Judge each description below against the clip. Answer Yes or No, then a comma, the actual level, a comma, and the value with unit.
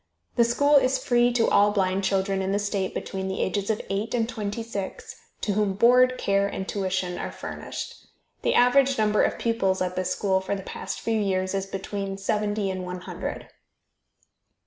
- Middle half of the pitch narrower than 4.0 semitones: Yes, average, 3.0 semitones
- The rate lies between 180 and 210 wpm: Yes, average, 190 wpm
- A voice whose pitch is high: Yes, high, 200 Hz